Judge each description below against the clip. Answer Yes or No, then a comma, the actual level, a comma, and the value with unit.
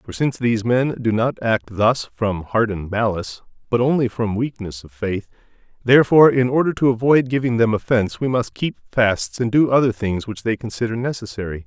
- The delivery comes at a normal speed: Yes, average, 190 wpm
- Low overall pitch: Yes, low, 115 Hz